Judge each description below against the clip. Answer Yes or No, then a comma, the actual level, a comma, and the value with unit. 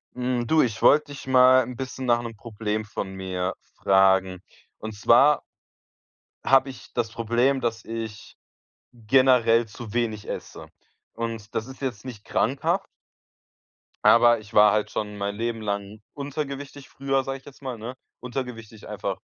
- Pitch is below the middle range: Yes, low, 115 Hz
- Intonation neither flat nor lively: Yes, average, 3.6 semitones